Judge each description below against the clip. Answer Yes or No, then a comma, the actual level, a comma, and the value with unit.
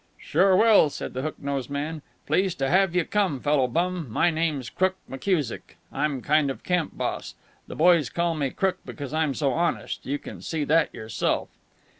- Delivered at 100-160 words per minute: No, average, 185 wpm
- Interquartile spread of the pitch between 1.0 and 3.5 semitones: No, average, 4.1 semitones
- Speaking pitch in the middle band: Yes, medium, 155 Hz